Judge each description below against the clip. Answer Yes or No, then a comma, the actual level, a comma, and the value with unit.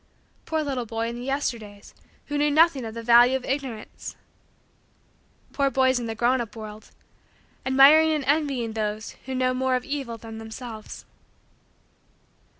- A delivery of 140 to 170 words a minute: Yes, average, 150 wpm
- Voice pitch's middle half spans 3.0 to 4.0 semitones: Yes, average, 3.4 semitones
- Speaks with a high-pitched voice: Yes, very high, 255 Hz